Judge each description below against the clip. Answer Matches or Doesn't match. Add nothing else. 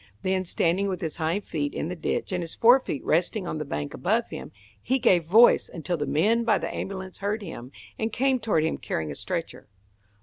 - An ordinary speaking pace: Doesn't match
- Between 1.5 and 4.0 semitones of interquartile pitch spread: Doesn't match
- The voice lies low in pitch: Doesn't match